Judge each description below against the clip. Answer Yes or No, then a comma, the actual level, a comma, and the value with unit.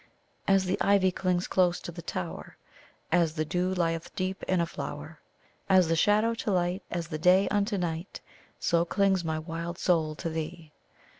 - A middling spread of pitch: No, narrow, 2.3 semitones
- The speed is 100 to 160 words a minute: No, average, 175 wpm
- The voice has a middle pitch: Yes, medium, 175 Hz